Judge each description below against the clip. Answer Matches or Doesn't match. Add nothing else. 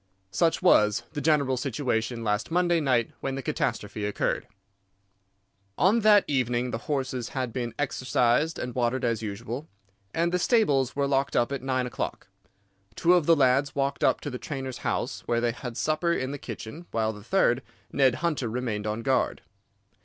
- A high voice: Doesn't match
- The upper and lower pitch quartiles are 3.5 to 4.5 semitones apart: Matches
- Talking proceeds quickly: Doesn't match